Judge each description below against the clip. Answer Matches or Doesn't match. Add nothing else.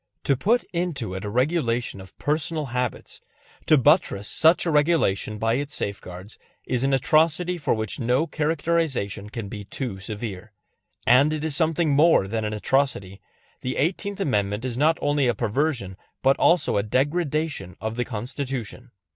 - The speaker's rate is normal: Matches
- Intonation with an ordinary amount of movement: Doesn't match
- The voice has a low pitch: Matches